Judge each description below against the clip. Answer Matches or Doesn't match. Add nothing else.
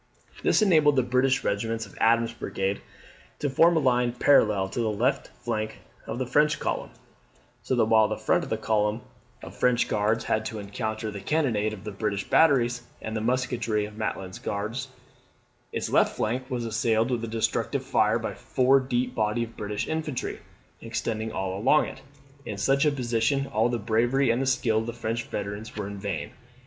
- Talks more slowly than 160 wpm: Doesn't match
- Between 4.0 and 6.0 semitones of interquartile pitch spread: Doesn't match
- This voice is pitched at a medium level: Doesn't match